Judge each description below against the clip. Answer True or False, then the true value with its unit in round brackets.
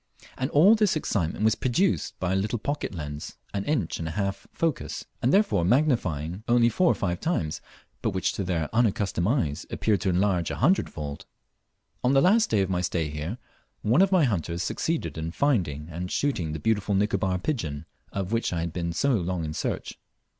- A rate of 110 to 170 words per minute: False (195 wpm)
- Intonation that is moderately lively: False (7.2 semitones)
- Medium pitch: False (100 Hz)